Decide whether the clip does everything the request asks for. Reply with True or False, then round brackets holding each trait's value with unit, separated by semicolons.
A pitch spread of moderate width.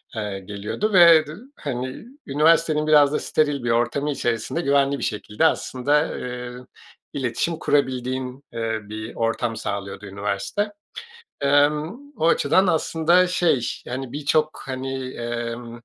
True (4.7 semitones)